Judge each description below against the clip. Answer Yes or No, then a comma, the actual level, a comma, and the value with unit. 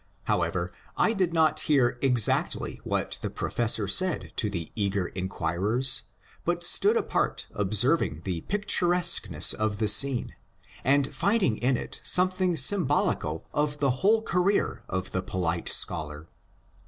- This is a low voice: Yes, low, 125 Hz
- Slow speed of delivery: Yes, slow, 130 wpm